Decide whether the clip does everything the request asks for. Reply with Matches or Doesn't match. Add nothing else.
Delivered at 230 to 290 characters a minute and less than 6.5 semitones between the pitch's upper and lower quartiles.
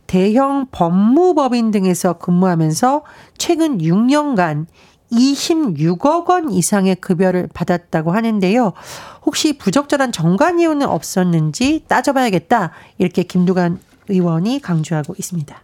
Doesn't match